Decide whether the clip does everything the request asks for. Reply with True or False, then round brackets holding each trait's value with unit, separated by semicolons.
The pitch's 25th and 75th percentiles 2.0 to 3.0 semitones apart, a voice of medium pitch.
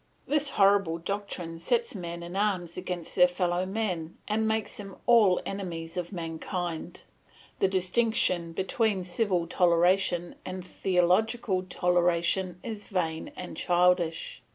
True (2.5 semitones; 180 Hz)